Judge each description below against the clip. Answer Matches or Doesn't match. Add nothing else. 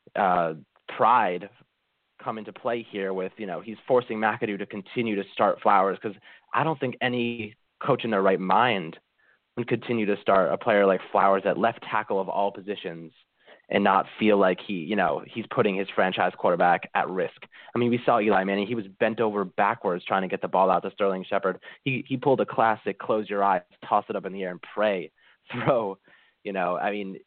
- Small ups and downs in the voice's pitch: Doesn't match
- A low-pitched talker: Matches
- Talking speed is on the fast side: Matches